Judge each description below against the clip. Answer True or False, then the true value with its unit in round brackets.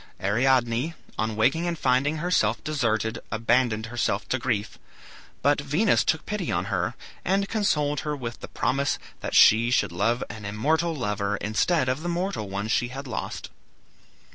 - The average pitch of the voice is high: False (125 Hz)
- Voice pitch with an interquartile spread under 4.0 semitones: False (5.4 semitones)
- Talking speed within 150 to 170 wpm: True (160 wpm)